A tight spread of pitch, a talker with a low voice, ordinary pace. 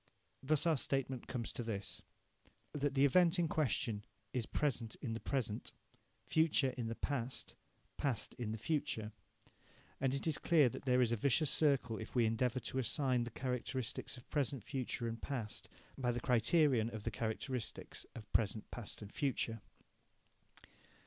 No: average, 3.5 semitones; low, 125 Hz; average, 160 wpm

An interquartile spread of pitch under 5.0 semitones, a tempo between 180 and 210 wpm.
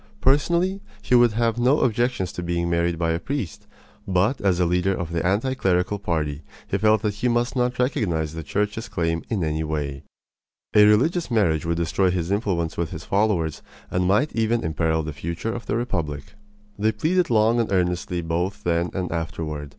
No: wide, 5.5 semitones; average, 190 wpm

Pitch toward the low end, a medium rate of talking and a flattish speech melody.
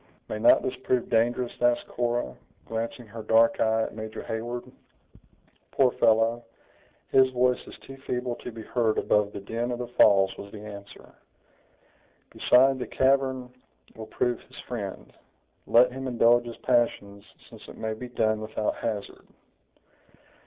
Yes: low, 120 Hz; average, 150 wpm; narrow, 2.2 semitones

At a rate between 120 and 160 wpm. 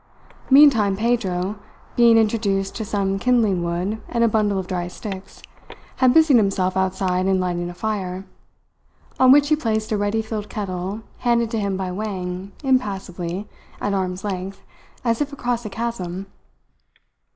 Yes: average, 150 wpm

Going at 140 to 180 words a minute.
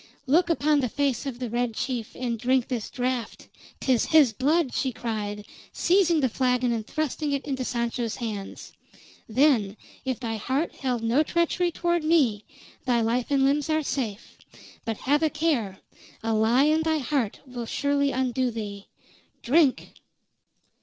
Yes: average, 160 wpm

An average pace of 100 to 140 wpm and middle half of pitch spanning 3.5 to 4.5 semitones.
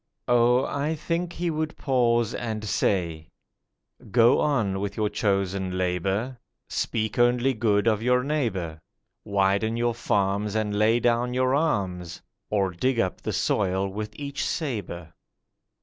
Yes: slow, 135 wpm; average, 4.2 semitones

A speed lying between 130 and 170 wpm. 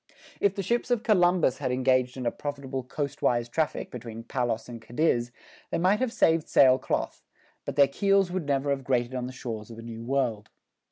No: average, 200 wpm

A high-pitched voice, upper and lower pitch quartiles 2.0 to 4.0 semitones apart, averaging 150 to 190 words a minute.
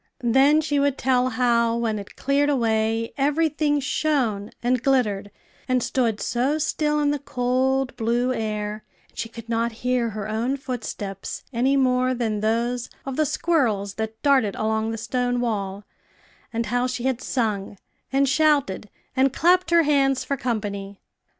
Yes: high, 245 Hz; average, 3.6 semitones; average, 160 wpm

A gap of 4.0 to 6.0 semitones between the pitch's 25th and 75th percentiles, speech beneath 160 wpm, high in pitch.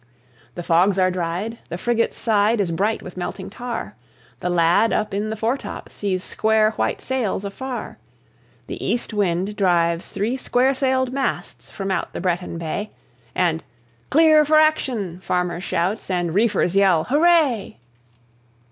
Yes: average, 5.1 semitones; average, 145 wpm; high, 205 Hz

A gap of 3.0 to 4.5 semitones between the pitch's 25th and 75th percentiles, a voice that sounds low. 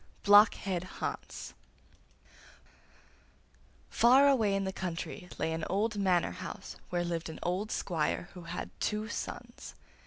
No: average, 3.3 semitones; high, 190 Hz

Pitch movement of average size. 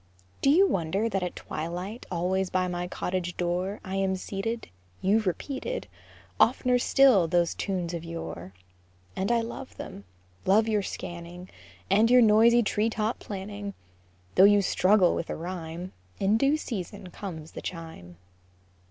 Yes: average, 3.9 semitones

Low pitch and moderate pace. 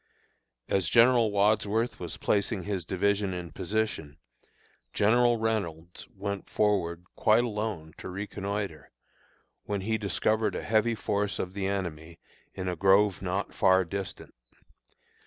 No: low, 100 Hz; slow, 125 wpm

